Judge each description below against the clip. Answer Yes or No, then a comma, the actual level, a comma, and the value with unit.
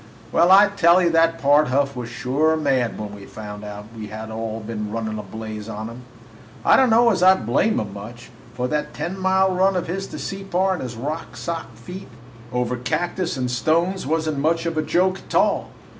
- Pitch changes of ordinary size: No, wide, 8.1 semitones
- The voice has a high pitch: No, medium, 145 Hz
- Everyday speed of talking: No, fast, 210 wpm